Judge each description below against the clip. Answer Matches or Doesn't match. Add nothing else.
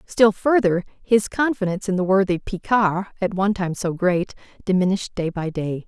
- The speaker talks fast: Doesn't match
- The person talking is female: Matches